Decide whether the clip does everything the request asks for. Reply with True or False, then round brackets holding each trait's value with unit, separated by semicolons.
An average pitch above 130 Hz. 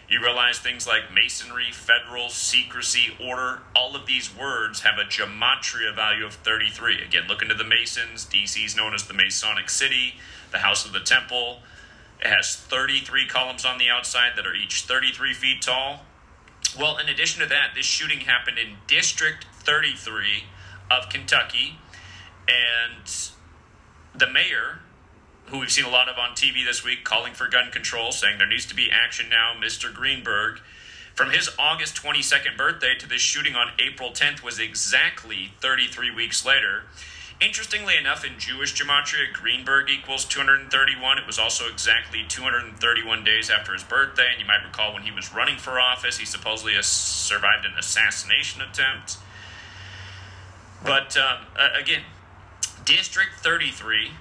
False (120 Hz)